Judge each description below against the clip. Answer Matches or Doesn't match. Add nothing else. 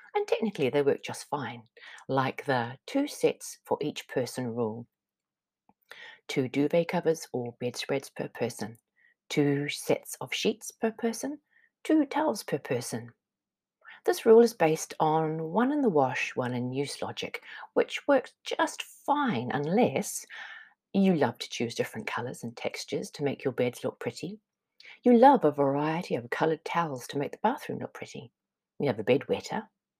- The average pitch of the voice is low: Doesn't match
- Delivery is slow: Doesn't match